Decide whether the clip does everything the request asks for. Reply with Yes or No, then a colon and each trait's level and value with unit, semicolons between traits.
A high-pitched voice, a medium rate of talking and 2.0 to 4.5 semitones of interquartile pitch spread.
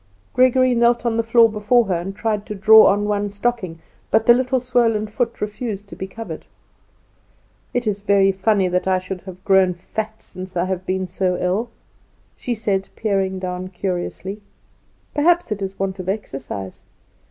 Yes: high, 205 Hz; average, 175 wpm; average, 3.4 semitones